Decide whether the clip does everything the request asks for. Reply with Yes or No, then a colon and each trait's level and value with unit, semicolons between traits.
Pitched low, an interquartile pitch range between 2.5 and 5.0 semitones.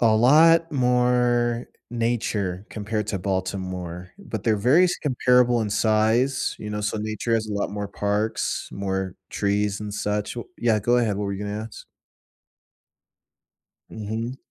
Yes: low, 110 Hz; average, 2.9 semitones